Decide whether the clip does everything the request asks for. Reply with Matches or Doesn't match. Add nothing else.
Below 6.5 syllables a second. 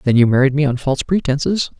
Doesn't match